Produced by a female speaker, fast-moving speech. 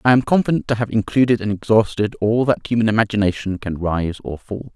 No: male; fast, 215 wpm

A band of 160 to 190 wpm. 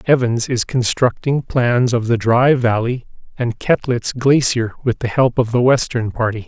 Yes: average, 165 wpm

